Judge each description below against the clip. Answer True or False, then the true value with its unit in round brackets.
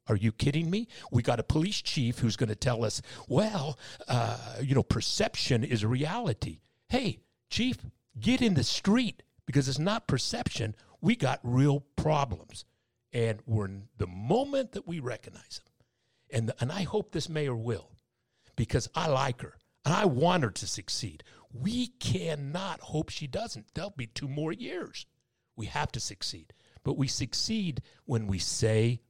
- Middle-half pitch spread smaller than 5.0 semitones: False (5.3 semitones)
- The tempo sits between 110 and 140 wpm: False (170 wpm)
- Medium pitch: False (125 Hz)